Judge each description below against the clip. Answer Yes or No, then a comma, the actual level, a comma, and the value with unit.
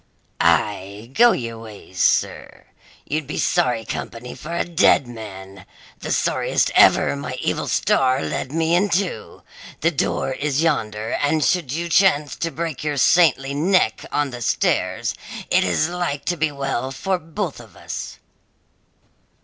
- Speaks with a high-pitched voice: No, medium, 140 Hz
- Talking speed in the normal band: Yes, average, 150 wpm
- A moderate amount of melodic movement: No, wide, 6.3 semitones